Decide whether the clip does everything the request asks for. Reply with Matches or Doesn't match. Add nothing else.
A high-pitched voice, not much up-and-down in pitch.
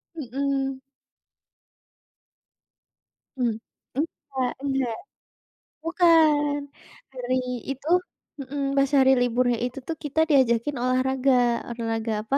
Matches